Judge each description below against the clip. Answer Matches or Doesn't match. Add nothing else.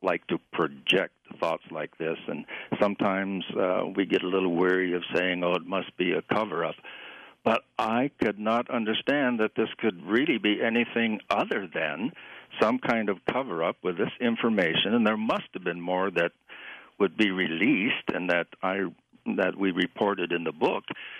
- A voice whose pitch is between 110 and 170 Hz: Doesn't match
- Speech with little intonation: Doesn't match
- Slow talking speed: Doesn't match